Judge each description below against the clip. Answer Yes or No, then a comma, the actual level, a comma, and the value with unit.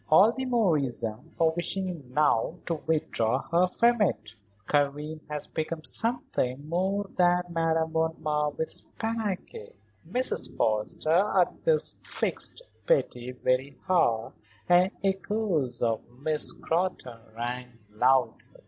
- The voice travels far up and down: Yes, wide, 6.5 semitones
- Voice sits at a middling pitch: Yes, medium, 160 Hz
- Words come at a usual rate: No, slow, 120 wpm